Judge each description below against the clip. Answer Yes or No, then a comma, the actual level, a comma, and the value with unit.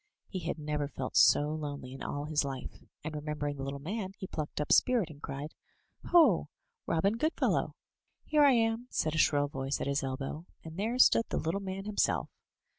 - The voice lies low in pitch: No, medium, 155 Hz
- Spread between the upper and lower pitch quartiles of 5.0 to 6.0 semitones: Yes, wide, 5.6 semitones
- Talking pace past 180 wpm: Yes, average, 195 wpm